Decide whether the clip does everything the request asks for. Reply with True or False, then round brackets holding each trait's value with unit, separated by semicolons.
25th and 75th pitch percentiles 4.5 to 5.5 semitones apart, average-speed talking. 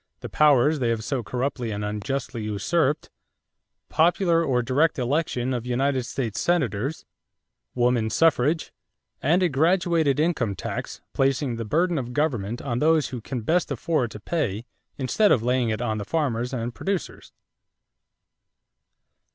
True (5.1 semitones; 145 wpm)